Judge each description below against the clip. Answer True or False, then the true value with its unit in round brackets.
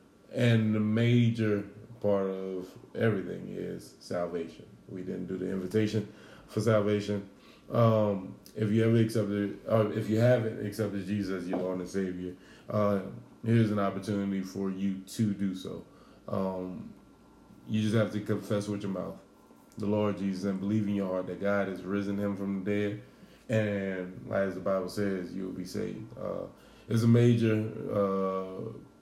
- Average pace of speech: True (160 wpm)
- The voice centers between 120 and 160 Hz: False (100 Hz)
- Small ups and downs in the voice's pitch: True (2.1 semitones)